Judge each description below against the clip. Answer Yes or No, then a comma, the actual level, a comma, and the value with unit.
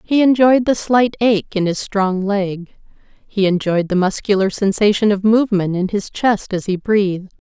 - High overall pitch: Yes, high, 205 Hz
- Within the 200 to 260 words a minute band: No, average, 175 wpm